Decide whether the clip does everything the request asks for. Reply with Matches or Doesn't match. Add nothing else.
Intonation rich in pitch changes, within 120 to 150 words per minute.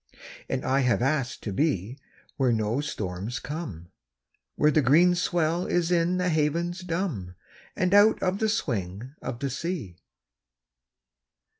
Matches